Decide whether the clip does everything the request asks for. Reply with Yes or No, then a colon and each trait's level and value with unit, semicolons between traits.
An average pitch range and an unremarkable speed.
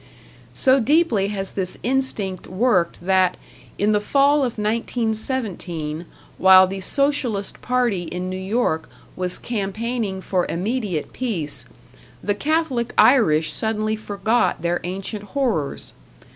No: average, 4.7 semitones; slow, 115 wpm